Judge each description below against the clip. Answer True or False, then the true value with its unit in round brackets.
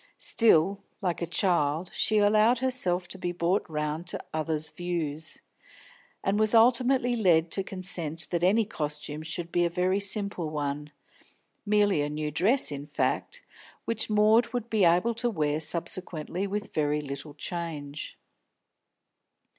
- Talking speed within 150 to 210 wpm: False (140 wpm)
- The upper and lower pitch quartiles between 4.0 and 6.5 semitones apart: True (5.2 semitones)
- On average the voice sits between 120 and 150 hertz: False (175 Hz)